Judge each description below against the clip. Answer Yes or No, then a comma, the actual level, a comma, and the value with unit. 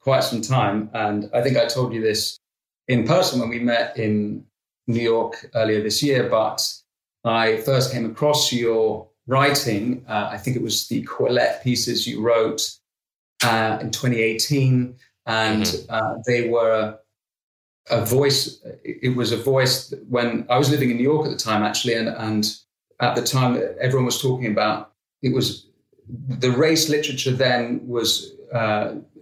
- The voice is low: Yes, low, 120 Hz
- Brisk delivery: No, average, 165 wpm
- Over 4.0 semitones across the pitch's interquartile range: No, average, 2.8 semitones